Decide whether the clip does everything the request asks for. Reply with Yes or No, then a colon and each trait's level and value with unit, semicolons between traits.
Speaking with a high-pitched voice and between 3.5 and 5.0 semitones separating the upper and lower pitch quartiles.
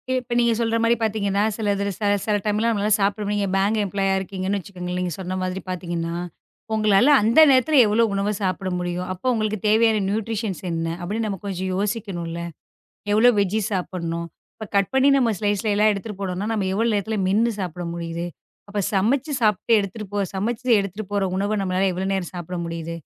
No: high, 200 Hz; average, 2.9 semitones